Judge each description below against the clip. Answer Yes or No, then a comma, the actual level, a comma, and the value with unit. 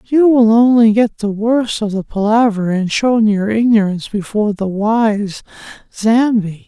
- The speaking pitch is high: Yes, high, 215 Hz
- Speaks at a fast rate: No, average, 160 wpm